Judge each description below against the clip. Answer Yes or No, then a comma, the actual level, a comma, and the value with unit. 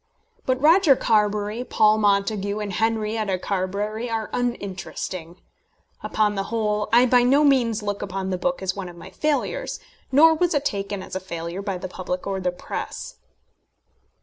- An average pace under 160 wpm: No, average, 165 wpm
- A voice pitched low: No, high, 210 Hz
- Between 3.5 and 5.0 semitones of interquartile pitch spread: Yes, average, 3.9 semitones